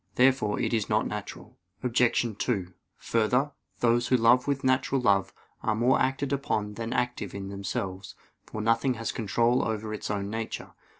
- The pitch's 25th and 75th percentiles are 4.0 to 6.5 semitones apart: No, average, 3.2 semitones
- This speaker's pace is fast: No, average, 165 wpm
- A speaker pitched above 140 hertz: No, low, 115 Hz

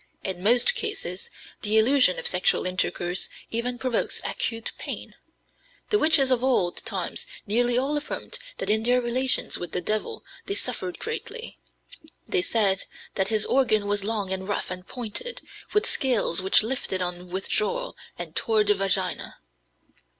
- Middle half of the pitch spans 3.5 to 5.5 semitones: Yes, average, 5.2 semitones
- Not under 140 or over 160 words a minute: Yes, average, 150 wpm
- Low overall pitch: No, high, 220 Hz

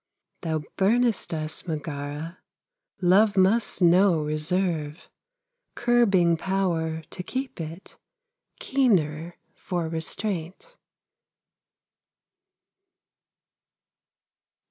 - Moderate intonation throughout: Yes, average, 3.7 semitones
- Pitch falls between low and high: Yes, medium, 175 Hz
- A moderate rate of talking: No, slow, 65 wpm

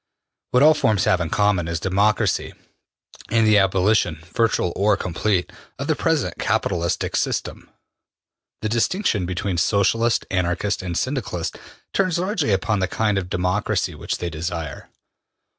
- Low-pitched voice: Yes, low, 100 Hz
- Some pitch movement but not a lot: Yes, average, 4.0 semitones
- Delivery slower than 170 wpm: Yes, average, 140 wpm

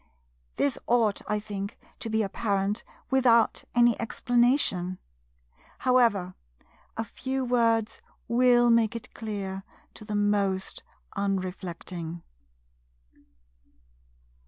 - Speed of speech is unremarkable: No, slow, 90 wpm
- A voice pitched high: Yes, high, 220 Hz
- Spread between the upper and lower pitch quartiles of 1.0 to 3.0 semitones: No, average, 3.4 semitones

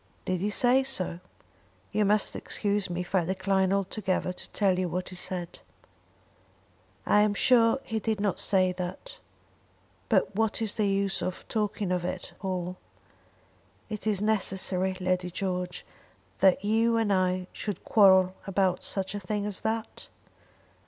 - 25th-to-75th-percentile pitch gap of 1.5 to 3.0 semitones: Yes, narrow, 2.4 semitones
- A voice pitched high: Yes, high, 195 Hz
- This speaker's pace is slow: No, average, 150 wpm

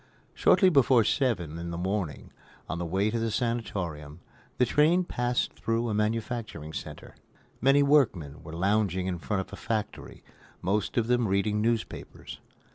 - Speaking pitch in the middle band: No, low, 105 Hz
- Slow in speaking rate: No, average, 155 wpm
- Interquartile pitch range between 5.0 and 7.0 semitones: Yes, average, 5.3 semitones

